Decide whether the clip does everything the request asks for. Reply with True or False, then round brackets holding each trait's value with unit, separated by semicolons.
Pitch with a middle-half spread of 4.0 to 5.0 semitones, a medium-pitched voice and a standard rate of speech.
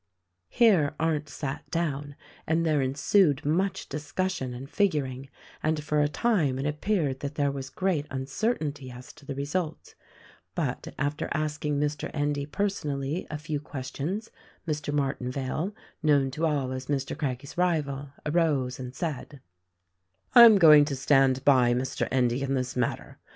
False (2.8 semitones; 145 Hz; 150 wpm)